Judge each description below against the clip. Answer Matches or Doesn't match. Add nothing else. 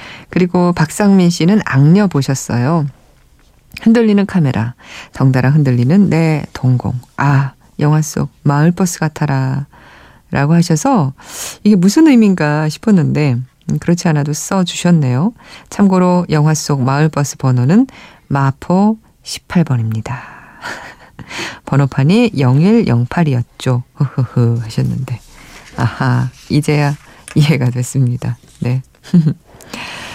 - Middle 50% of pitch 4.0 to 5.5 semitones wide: Matches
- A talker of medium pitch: Matches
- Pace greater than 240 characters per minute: Doesn't match